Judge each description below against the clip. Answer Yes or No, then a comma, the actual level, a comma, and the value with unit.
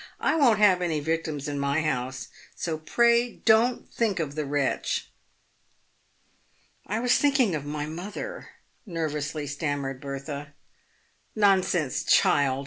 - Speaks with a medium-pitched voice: Yes, medium, 155 Hz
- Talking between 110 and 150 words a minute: Yes, slow, 135 wpm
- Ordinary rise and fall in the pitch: No, wide, 6.4 semitones